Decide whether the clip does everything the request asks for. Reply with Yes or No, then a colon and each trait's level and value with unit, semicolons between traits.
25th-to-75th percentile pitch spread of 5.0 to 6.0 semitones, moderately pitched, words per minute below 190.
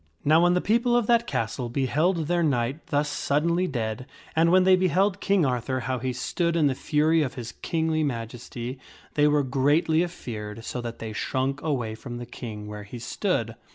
No: wide, 5.6 semitones; medium, 145 Hz; average, 195 wpm